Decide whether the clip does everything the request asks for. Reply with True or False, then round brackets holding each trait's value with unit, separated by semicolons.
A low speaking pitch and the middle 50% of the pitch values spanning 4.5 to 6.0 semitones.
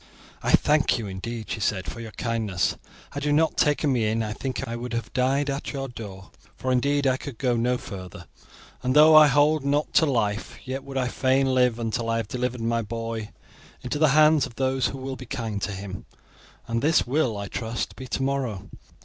False (125 Hz; 3.4 semitones)